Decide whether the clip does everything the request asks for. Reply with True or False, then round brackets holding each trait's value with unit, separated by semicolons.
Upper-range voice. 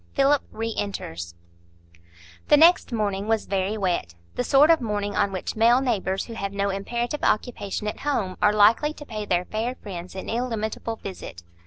True (210 Hz)